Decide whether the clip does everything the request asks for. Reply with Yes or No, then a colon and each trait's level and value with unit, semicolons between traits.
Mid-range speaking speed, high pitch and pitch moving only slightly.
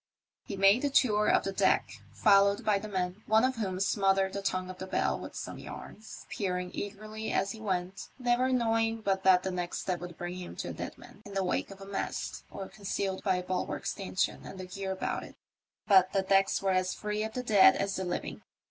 No: fast, 230 wpm; high, 195 Hz; narrow, 2.2 semitones